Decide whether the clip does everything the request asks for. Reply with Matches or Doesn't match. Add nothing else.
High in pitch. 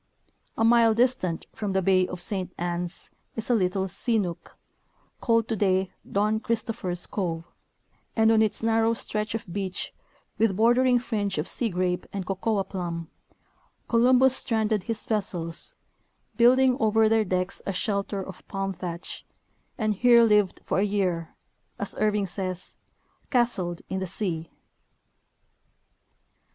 Matches